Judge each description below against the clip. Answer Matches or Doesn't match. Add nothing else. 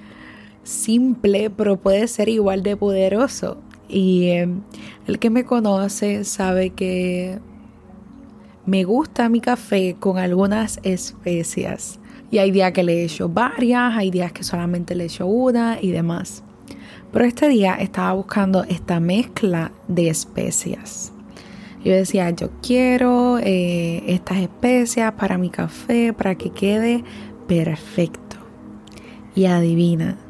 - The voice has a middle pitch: Doesn't match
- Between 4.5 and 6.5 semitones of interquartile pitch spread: Doesn't match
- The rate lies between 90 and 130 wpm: Matches